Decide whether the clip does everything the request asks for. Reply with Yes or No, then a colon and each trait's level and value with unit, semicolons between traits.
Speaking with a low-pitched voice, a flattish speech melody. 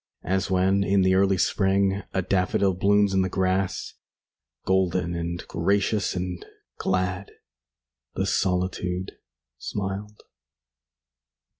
Yes: very low, 95 Hz; narrow, 1.2 semitones